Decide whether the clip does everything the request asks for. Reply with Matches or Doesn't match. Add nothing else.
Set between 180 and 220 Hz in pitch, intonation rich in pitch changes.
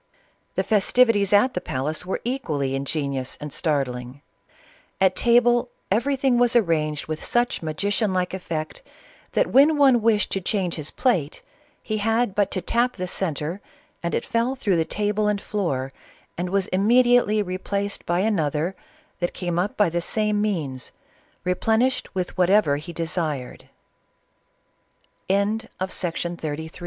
Matches